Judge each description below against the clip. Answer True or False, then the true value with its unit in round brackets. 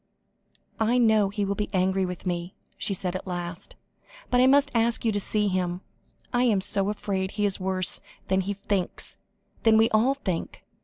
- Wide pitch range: False (2.9 semitones)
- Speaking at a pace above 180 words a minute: True (190 wpm)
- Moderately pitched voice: False (200 Hz)